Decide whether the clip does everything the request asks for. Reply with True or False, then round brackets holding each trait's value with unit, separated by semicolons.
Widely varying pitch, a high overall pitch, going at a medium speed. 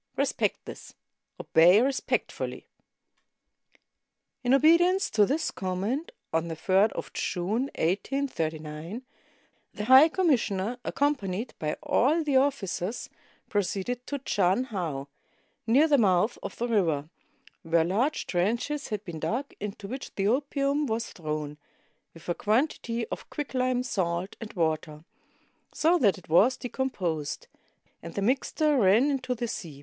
False (7.1 semitones; 215 Hz; 130 wpm)